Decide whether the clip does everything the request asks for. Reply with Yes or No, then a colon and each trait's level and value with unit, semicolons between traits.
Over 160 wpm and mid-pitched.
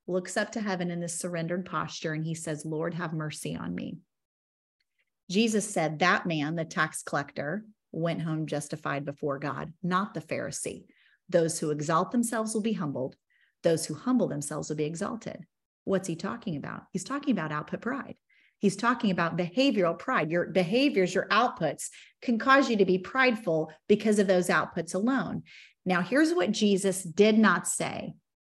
Yes: average, 170 wpm; medium, 180 Hz